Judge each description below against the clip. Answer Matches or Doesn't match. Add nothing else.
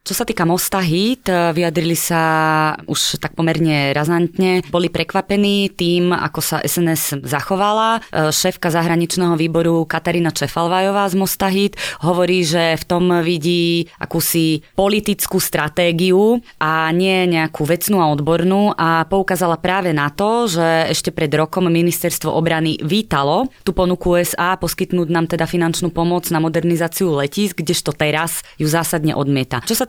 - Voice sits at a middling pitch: Matches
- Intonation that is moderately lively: Doesn't match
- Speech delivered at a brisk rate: Doesn't match